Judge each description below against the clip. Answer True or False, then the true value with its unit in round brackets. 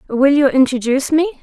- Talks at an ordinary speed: True (170 wpm)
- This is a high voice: True (275 Hz)